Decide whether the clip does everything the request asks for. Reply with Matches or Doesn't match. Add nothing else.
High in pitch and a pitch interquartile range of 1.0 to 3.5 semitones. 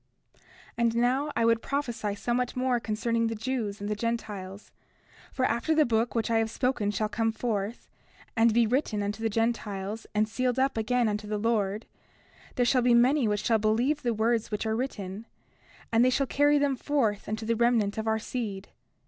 Matches